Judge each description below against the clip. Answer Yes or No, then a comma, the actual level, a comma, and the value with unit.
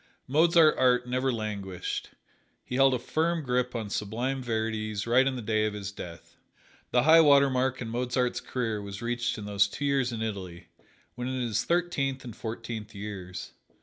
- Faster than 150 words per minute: Yes, average, 180 wpm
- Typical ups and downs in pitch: Yes, average, 3.7 semitones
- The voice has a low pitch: Yes, low, 120 Hz